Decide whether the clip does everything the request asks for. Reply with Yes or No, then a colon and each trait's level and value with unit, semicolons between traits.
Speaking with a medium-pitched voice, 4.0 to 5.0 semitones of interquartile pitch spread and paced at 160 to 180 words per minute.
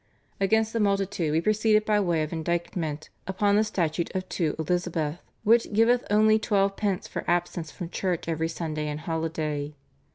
Yes: medium, 175 Hz; average, 4.5 semitones; average, 165 wpm